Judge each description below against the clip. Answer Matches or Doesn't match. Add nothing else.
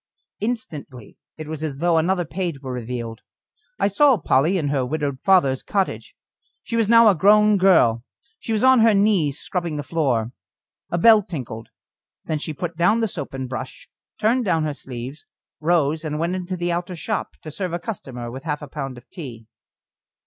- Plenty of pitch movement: Matches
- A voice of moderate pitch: Matches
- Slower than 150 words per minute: Doesn't match